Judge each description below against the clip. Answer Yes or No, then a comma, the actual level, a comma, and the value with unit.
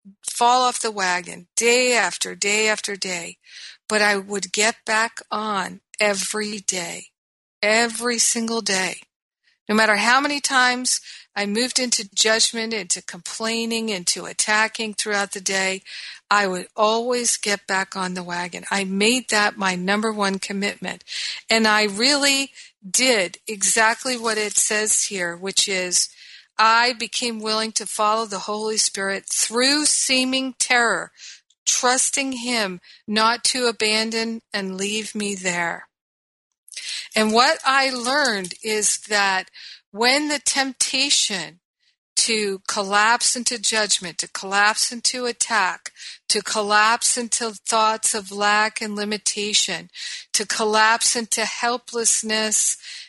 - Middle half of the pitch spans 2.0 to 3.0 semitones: Yes, average, 2.7 semitones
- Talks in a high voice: Yes, high, 220 Hz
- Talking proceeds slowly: Yes, slow, 125 wpm